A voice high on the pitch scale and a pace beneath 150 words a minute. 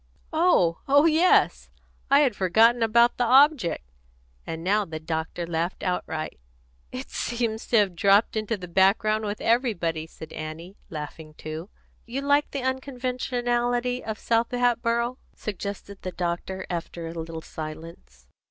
Yes: high, 210 Hz; average, 140 wpm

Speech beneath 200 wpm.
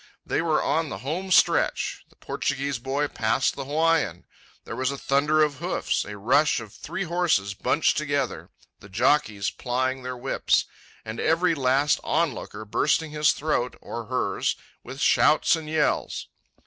Yes: average, 160 wpm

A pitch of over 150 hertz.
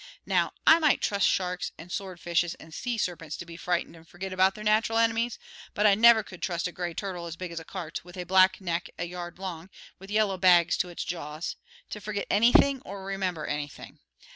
Yes: medium, 185 Hz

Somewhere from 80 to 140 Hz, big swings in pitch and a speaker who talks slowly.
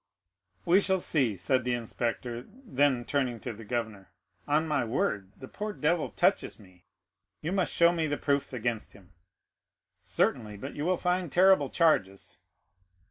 No: low, 135 Hz; wide, 6.8 semitones; average, 155 wpm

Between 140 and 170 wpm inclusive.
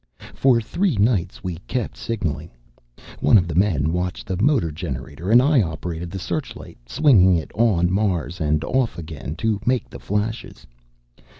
Yes: average, 160 wpm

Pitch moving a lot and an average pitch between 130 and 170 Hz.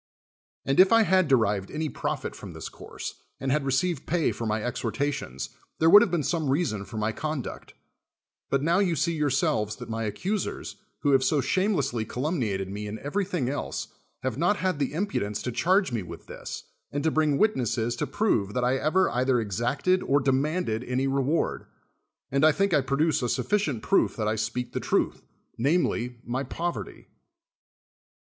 Yes: wide, 5.8 semitones; medium, 140 Hz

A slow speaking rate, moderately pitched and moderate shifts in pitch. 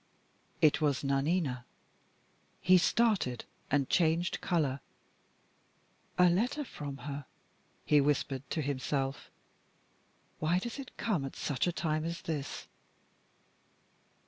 Yes: slow, 110 wpm; medium, 155 Hz; average, 4.2 semitones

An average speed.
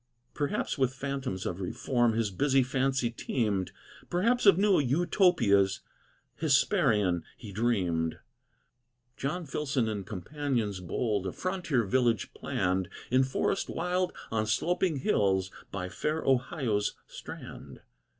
No: slow, 115 wpm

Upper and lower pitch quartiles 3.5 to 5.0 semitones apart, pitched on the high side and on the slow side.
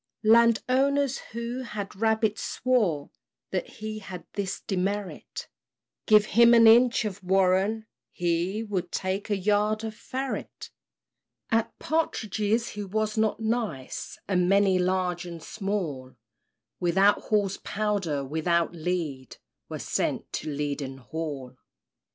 Yes: average, 3.9 semitones; high, 200 Hz; slow, 120 wpm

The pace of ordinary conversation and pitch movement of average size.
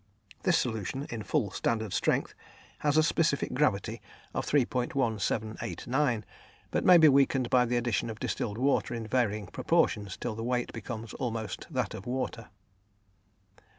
Yes: average, 145 wpm; average, 3.4 semitones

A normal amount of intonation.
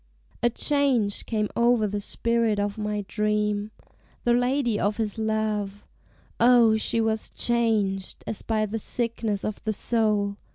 No: narrow, 2.0 semitones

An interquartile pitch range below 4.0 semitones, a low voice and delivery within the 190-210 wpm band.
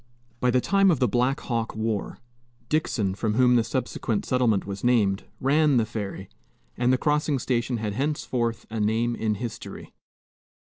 No: average, 2.9 semitones; low, 120 Hz; average, 160 wpm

